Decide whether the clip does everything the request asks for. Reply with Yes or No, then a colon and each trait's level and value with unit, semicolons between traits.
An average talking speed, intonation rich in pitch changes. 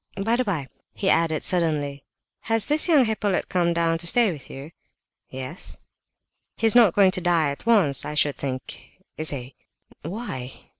Yes: average, 165 wpm; wide, 6.4 semitones